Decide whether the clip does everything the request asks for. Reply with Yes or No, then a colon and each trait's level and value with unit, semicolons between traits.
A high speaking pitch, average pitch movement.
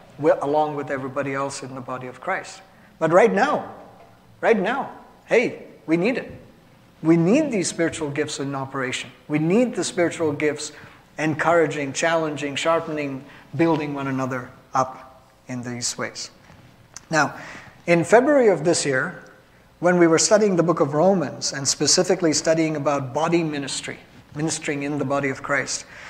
No: medium, 150 Hz; average, 3.2 semitones